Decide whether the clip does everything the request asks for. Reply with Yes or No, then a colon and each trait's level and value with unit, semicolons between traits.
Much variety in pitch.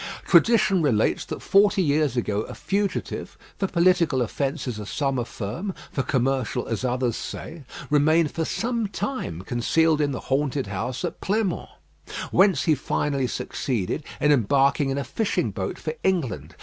Yes: wide, 5.8 semitones